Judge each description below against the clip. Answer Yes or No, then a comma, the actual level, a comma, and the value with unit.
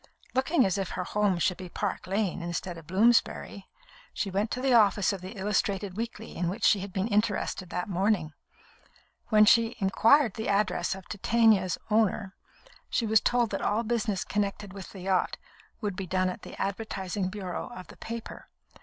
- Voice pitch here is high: Yes, high, 200 Hz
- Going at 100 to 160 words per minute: No, average, 180 wpm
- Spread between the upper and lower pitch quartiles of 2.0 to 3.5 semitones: Yes, average, 2.9 semitones